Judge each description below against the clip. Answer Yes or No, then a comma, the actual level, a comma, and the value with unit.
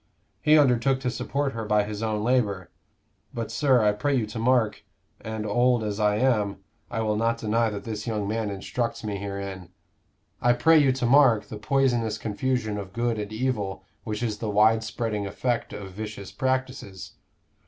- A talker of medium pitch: No, low, 110 Hz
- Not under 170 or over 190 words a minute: Yes, average, 180 wpm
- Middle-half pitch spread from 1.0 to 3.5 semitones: Yes, average, 2.9 semitones